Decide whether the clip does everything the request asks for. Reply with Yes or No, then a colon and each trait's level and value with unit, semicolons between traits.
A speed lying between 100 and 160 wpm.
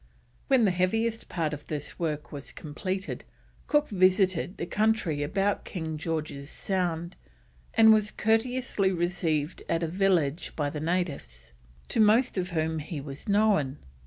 Yes: average, 145 wpm